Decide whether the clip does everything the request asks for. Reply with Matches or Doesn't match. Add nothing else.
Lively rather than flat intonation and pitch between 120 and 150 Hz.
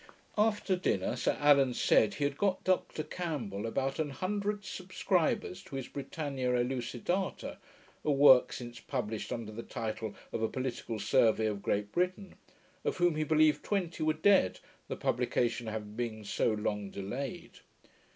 Matches